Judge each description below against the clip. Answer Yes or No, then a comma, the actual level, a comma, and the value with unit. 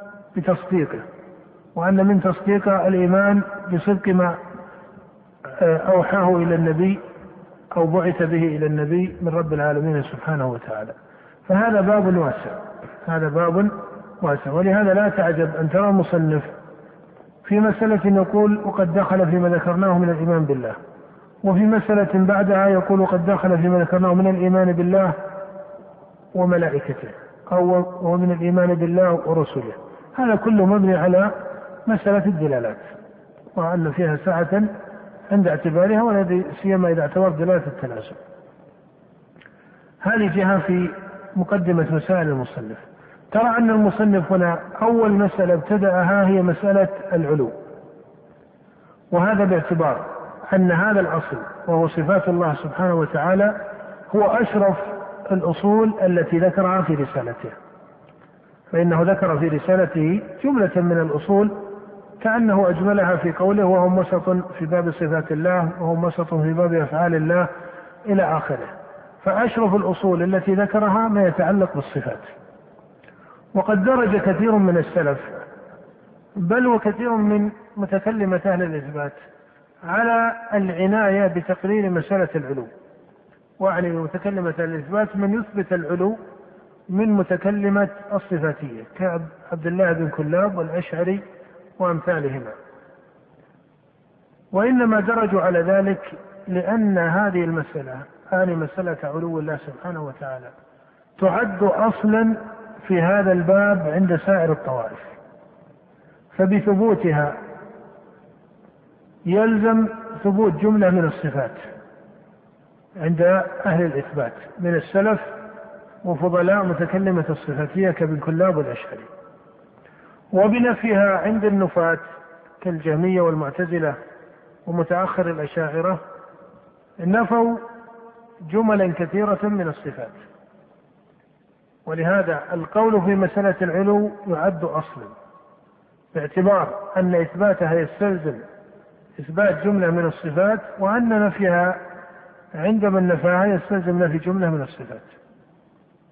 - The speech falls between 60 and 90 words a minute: No, average, 100 wpm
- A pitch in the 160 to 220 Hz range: Yes, medium, 185 Hz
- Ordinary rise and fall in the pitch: Yes, average, 3.0 semitones